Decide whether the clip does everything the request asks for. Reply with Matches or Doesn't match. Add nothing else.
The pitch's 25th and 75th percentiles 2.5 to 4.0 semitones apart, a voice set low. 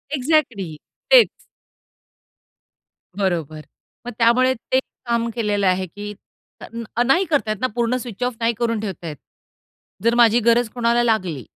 Doesn't match